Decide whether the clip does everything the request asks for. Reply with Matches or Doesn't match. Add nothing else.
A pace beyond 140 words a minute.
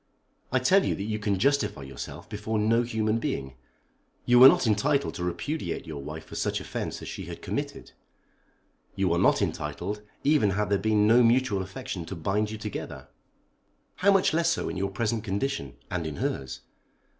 Matches